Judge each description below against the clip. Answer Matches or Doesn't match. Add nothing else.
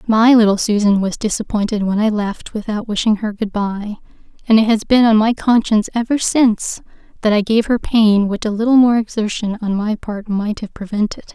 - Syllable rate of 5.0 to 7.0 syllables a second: Matches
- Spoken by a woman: Matches